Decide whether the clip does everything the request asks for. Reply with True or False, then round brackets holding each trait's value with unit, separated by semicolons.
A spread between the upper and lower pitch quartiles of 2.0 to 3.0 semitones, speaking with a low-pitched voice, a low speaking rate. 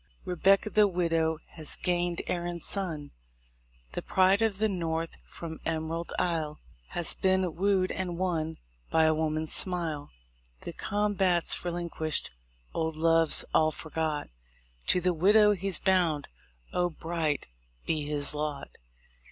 False (2.7 semitones; 170 Hz; 125 wpm)